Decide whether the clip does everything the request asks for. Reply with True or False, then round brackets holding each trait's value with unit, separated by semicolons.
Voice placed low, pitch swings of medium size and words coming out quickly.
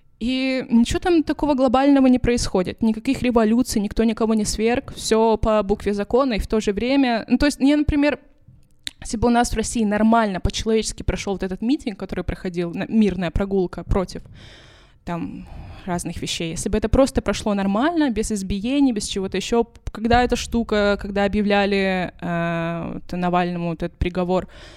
False (220 Hz; 4.1 semitones; 170 wpm)